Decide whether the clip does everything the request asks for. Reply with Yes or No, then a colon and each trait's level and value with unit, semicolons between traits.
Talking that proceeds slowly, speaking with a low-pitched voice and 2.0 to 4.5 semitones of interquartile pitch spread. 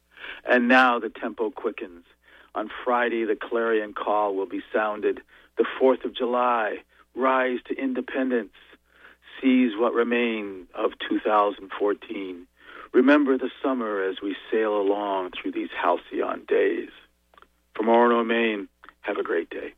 Yes: slow, 130 wpm; low, 120 Hz; average, 3.9 semitones